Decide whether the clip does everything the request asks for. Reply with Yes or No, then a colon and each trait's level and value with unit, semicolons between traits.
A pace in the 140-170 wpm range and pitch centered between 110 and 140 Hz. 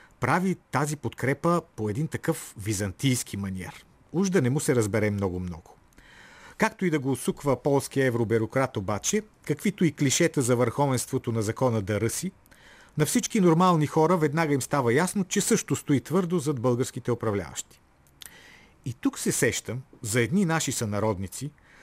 Yes: average, 150 wpm; low, 135 Hz